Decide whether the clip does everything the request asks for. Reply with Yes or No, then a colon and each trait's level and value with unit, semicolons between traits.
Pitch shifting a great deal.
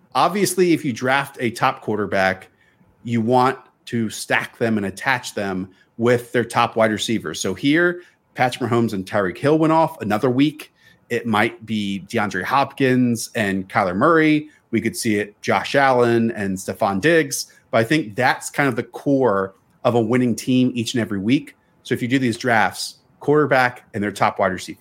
No: average, 3.8 semitones